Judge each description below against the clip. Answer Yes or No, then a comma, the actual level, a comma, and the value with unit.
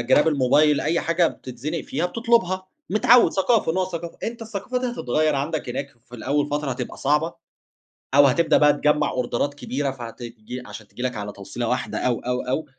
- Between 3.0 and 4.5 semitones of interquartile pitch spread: No, average, 5.2 semitones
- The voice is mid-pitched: Yes, medium, 150 Hz